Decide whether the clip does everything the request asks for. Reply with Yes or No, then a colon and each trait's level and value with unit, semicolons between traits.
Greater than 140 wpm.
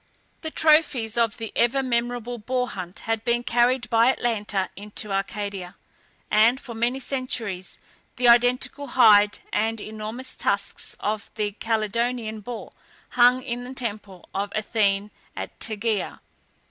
No: slow, 135 wpm